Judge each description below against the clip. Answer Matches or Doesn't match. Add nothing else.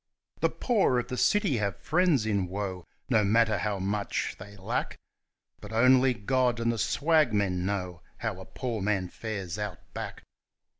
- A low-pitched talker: Matches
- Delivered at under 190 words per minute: Matches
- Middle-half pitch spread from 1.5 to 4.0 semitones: Doesn't match